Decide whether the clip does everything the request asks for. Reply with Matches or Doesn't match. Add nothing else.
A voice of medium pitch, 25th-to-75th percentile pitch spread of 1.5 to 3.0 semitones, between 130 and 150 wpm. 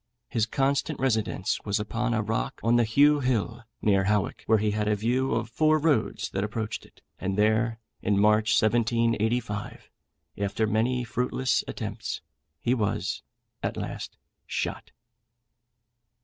Doesn't match